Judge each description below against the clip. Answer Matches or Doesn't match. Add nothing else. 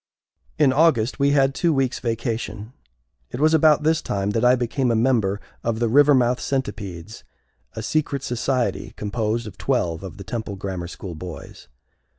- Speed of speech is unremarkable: Matches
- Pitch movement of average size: Matches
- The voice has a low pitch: Matches